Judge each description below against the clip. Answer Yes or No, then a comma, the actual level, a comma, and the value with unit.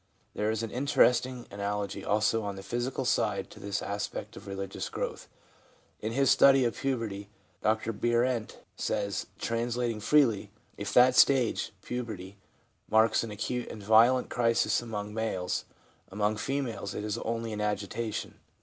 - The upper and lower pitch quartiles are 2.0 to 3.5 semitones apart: Yes, average, 2.9 semitones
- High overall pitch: No, low, 110 Hz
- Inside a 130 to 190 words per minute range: Yes, average, 150 wpm